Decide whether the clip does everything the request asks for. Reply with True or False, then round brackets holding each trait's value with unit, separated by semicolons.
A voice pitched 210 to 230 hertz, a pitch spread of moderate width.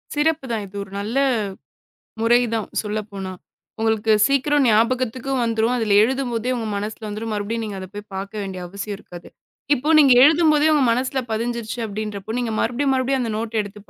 True (225 Hz; 3.5 semitones)